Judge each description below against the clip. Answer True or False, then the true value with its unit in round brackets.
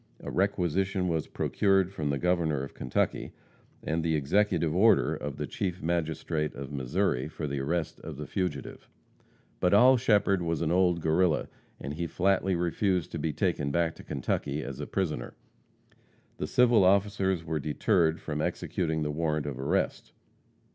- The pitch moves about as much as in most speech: True (3.9 semitones)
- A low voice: True (85 Hz)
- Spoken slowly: False (160 wpm)